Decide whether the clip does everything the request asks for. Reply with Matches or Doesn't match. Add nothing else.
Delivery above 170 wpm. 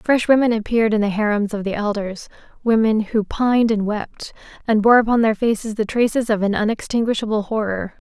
Matches